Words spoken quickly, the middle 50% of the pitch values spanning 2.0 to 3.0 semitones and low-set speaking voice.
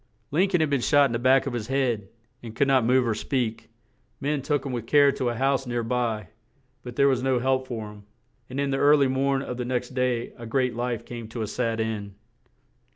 Yes: fast, 240 wpm; average, 2.7 semitones; low, 125 Hz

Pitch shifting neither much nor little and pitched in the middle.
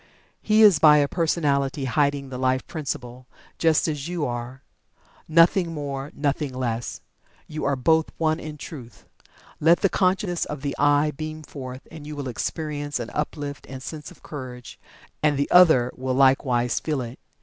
Yes: average, 3.2 semitones; medium, 145 Hz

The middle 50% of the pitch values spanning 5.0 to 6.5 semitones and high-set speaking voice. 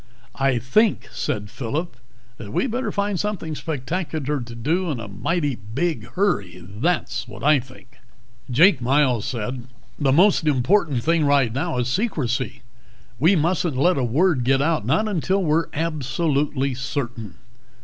No: wide, 5.6 semitones; medium, 145 Hz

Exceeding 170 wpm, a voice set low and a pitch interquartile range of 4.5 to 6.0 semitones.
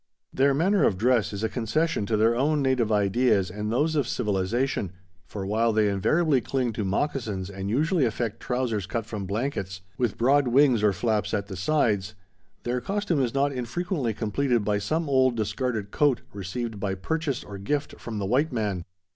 Yes: average, 180 wpm; low, 115 Hz; average, 5.0 semitones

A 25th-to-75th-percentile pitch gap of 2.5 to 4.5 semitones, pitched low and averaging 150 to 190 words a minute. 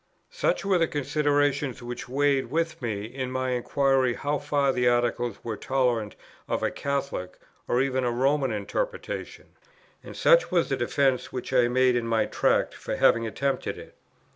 Yes: average, 2.9 semitones; low, 130 Hz; average, 165 wpm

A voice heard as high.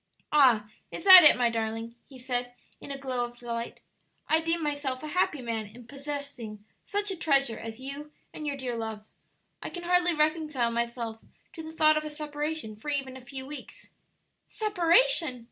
Yes: very high, 275 Hz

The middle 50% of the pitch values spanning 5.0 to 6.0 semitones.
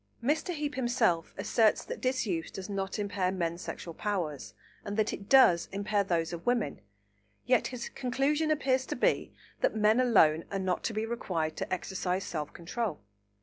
Yes: wide, 5.6 semitones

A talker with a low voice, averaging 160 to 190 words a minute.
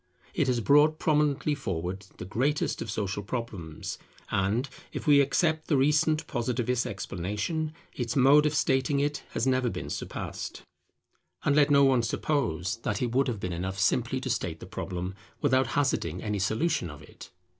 Yes: low, 125 Hz; average, 165 wpm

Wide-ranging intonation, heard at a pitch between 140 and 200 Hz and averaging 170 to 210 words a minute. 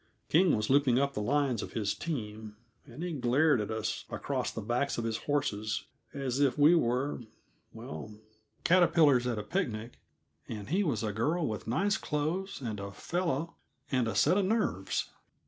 No: wide, 6.4 semitones; low, 130 Hz; average, 175 wpm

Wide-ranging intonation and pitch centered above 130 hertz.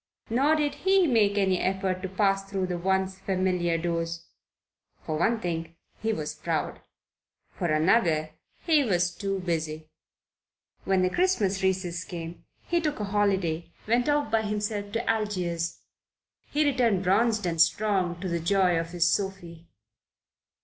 No: average, 3.7 semitones; high, 190 Hz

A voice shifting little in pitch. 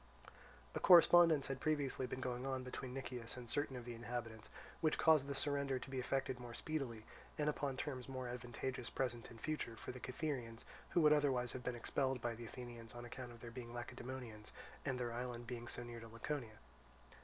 Yes: narrow, 2.2 semitones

